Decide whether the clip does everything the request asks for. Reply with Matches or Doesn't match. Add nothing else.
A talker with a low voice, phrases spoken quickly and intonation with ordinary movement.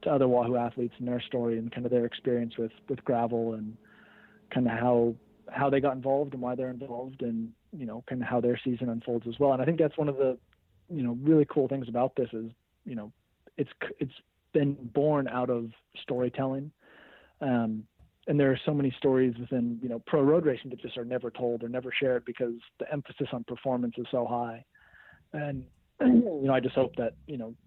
Doesn't match